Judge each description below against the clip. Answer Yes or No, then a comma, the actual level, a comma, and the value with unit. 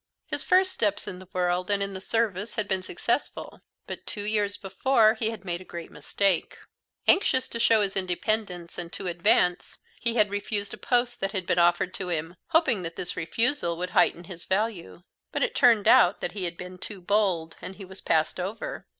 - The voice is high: Yes, high, 195 Hz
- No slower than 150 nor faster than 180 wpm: No, average, 200 wpm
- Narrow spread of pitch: No, average, 3.6 semitones